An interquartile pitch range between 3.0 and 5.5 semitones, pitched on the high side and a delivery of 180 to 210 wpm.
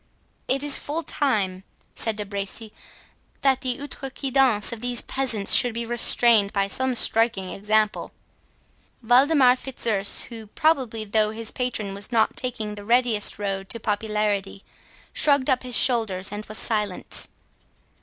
No: average, 3.6 semitones; high, 225 Hz; average, 145 wpm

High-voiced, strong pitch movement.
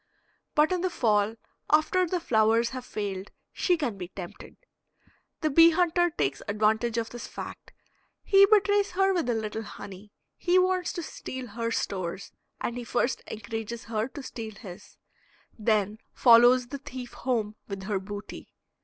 Yes: high, 235 Hz; wide, 6.9 semitones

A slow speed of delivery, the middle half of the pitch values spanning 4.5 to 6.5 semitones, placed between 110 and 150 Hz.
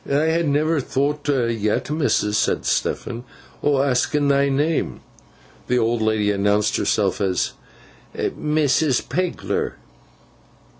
Yes: slow, 110 wpm; average, 5.2 semitones; low, 135 Hz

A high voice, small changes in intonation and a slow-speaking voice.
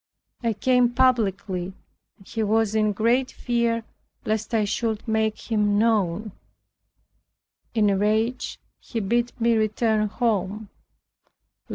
Yes: high, 220 Hz; narrow, 2.0 semitones; slow, 120 wpm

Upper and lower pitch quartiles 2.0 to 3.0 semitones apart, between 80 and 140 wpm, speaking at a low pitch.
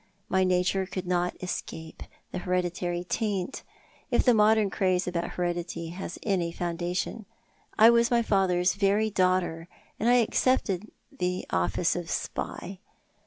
No: narrow, 2.5 semitones; slow, 135 wpm; medium, 185 Hz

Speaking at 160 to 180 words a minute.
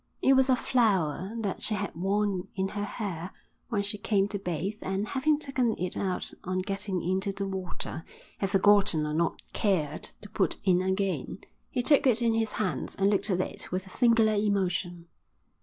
No: average, 190 wpm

